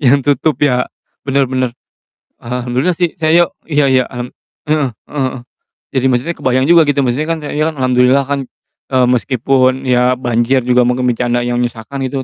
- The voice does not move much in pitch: Yes, narrow, 2.3 semitones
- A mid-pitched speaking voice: No, low, 130 Hz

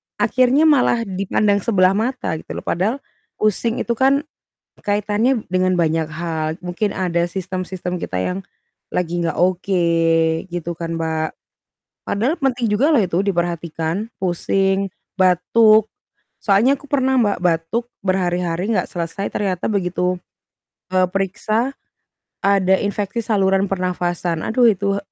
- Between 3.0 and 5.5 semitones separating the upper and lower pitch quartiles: Yes, average, 3.6 semitones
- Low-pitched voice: No, high, 190 Hz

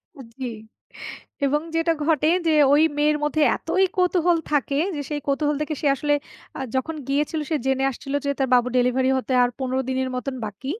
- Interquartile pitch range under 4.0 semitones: Yes, average, 2.7 semitones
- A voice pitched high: Yes, very high, 280 Hz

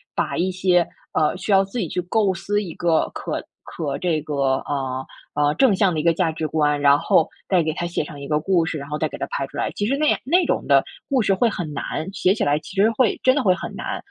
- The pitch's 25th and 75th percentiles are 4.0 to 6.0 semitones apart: Yes, average, 4.5 semitones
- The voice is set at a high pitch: No, medium, 170 Hz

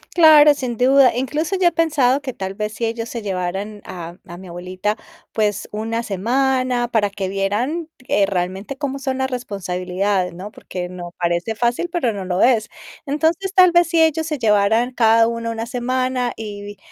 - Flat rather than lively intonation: No, average, 5.2 semitones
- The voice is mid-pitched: No, high, 230 Hz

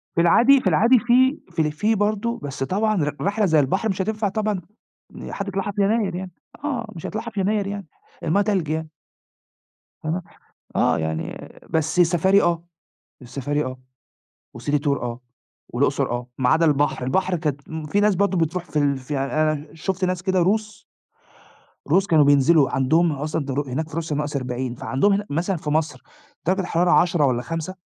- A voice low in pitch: No, medium, 170 Hz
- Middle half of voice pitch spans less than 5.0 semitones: No, average, 5.3 semitones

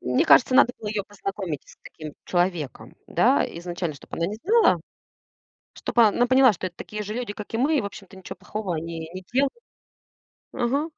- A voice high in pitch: Yes, high, 205 Hz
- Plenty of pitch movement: Yes, wide, 5.8 semitones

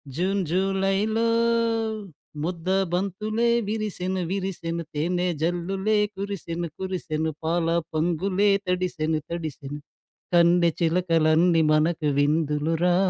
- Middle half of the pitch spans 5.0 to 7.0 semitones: No, average, 2.9 semitones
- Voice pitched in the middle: Yes, medium, 175 Hz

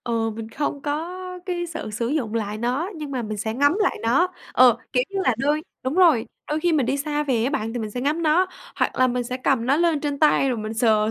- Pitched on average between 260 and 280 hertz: Yes, very high, 265 Hz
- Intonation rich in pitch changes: No, average, 4.9 semitones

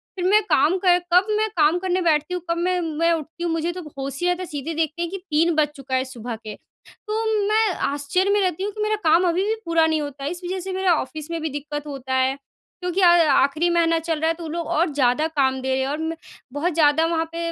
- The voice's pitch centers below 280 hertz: No, very high, 330 Hz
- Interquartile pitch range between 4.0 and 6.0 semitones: No, average, 3.3 semitones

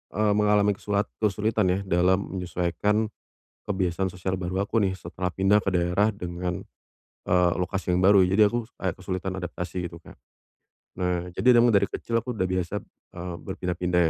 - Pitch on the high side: No, very low, 95 Hz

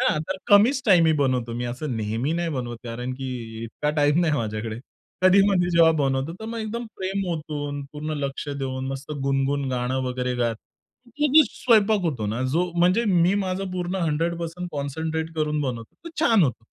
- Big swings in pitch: Yes, wide, 5.8 semitones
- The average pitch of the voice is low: No, medium, 150 Hz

